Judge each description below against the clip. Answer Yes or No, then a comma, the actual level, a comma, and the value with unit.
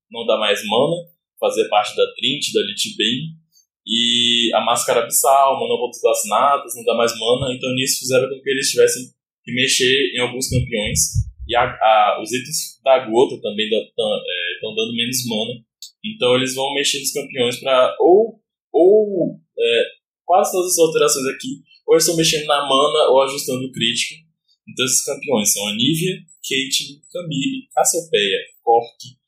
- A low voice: No, medium, 160 Hz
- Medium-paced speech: Yes, average, 170 wpm